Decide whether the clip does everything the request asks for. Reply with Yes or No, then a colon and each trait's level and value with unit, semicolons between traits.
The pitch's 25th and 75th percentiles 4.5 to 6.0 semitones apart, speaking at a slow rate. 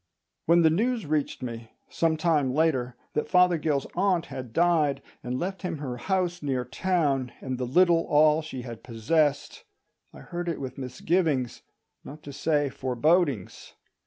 No: average, 4.9 semitones; average, 155 wpm